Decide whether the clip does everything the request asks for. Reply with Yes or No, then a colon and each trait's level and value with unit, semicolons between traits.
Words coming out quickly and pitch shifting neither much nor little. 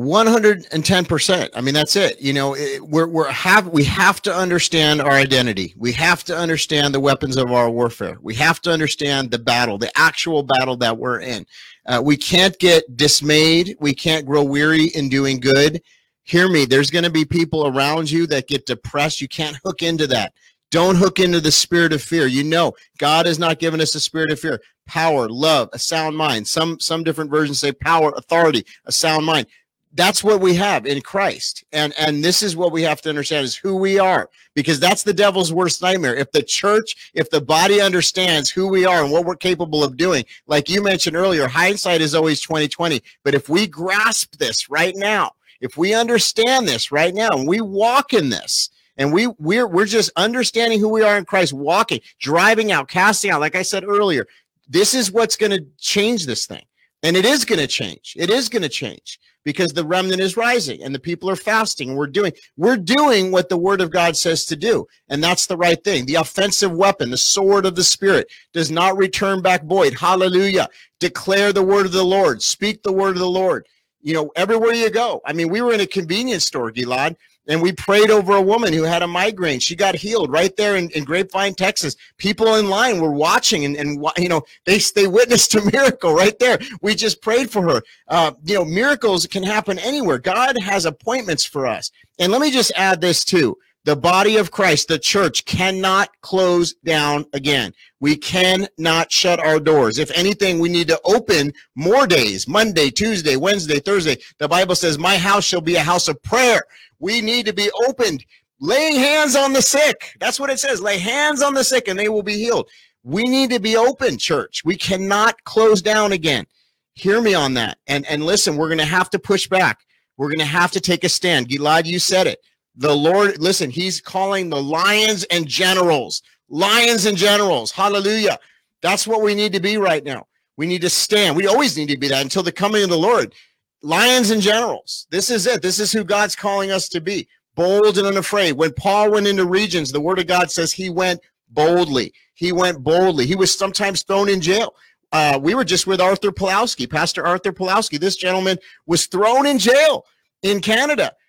Yes: fast, 210 wpm; average, 4.4 semitones